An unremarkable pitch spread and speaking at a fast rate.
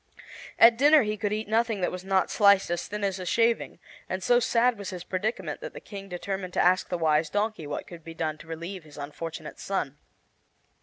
Yes: average, 4.2 semitones; fast, 215 wpm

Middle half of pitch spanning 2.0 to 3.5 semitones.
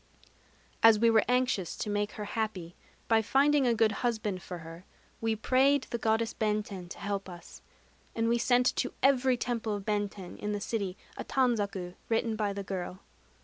Yes: average, 2.9 semitones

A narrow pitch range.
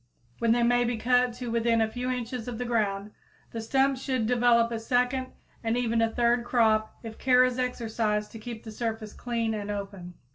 Yes: narrow, 1.9 semitones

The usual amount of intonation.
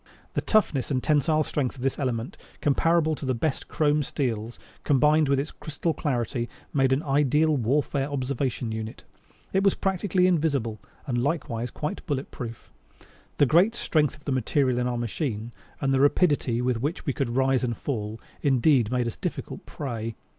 Yes: average, 3.7 semitones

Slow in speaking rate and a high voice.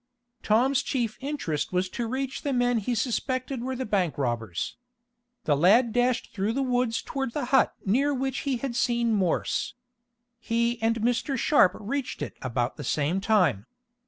No: average, 165 wpm; high, 235 Hz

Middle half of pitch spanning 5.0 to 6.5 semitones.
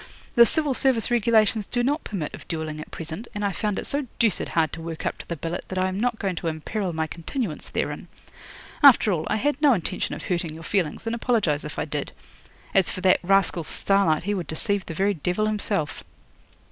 Yes: wide, 5.4 semitones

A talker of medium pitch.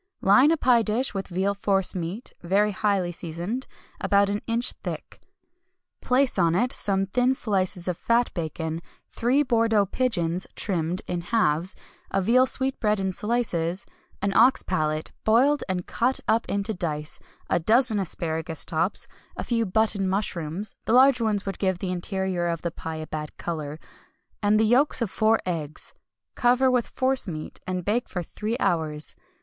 No: high, 195 Hz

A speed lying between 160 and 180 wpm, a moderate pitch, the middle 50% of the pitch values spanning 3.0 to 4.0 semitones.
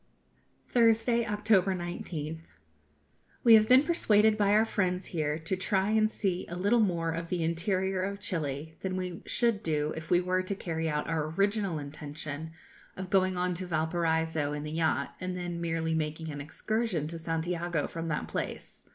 Yes: average, 175 wpm; medium, 175 Hz; average, 3.6 semitones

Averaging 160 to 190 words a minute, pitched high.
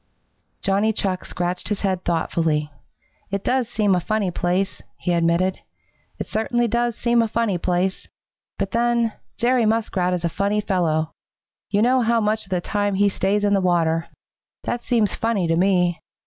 Yes: average, 170 wpm; high, 195 Hz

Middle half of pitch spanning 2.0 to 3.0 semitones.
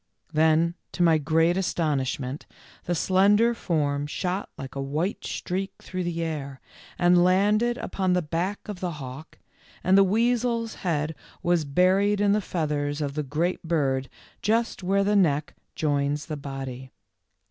No: average, 4.8 semitones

